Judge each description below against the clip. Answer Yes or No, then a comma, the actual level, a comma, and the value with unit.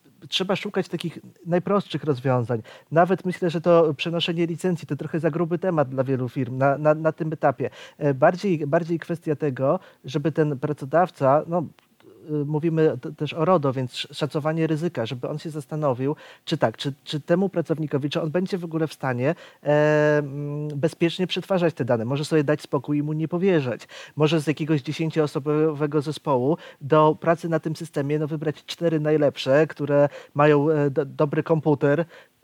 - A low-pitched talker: No, medium, 155 Hz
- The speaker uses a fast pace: Yes, fast, 165 wpm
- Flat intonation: Yes, narrow, 2.3 semitones